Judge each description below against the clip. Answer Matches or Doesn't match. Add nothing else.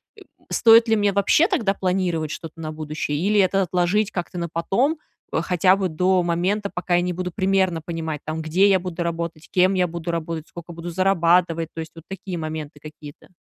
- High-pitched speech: Doesn't match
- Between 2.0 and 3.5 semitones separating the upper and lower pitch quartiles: Matches